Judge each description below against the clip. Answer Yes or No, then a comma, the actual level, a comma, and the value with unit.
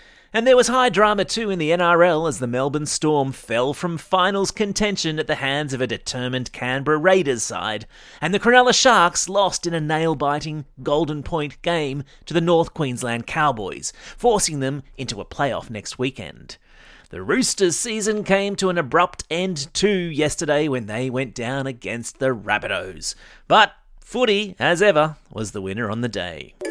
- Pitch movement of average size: No, wide, 6.2 semitones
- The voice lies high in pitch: No, medium, 155 Hz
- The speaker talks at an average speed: Yes, average, 170 wpm